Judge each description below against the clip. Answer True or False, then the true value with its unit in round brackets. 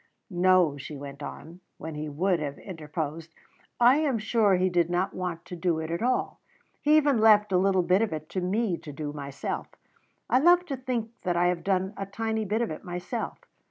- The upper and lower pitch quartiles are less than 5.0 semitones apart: False (5.3 semitones)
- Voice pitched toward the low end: False (185 Hz)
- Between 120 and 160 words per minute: False (205 wpm)